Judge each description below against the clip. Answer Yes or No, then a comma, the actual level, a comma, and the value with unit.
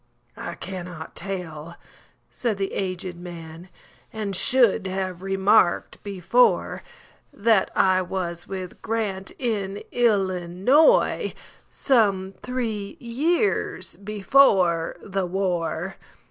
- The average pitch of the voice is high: Yes, high, 195 Hz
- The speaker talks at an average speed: No, slow, 75 wpm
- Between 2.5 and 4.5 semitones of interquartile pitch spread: Yes, average, 3.5 semitones